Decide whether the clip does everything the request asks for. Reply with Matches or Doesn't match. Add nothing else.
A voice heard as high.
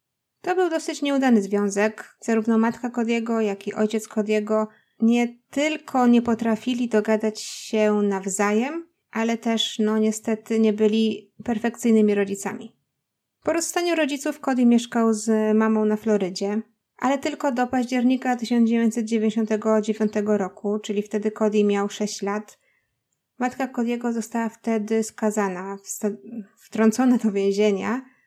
Matches